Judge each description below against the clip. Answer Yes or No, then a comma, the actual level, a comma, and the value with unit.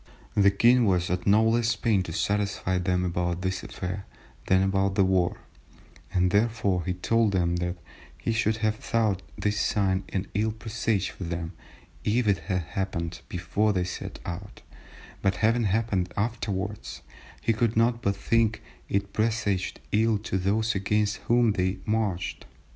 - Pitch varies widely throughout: No, average, 3.2 semitones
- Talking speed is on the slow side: No, average, 160 wpm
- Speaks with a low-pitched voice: Yes, low, 100 Hz